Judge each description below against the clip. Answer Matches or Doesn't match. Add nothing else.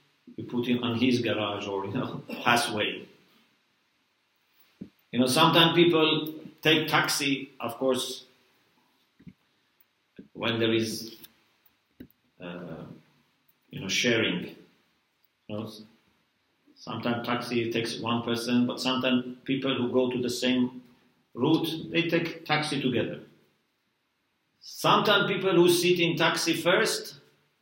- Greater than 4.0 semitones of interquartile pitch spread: Matches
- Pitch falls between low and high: Doesn't match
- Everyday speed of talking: Doesn't match